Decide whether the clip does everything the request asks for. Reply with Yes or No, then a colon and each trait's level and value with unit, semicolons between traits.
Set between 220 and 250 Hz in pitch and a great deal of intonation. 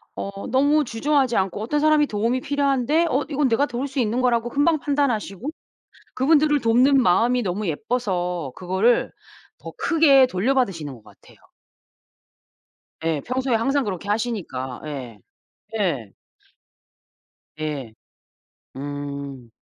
Yes: high, 230 Hz; wide, 7.5 semitones